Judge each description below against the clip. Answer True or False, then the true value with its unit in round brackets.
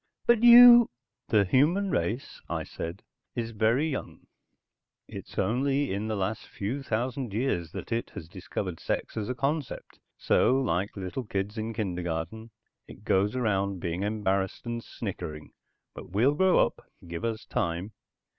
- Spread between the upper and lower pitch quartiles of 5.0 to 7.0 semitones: True (5.3 semitones)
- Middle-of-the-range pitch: False (110 Hz)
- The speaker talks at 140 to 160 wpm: True (150 wpm)